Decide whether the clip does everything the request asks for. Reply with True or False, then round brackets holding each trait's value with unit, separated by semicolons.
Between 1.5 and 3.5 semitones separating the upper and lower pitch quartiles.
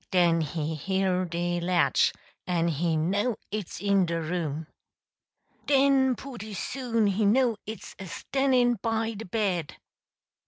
False (5.0 semitones)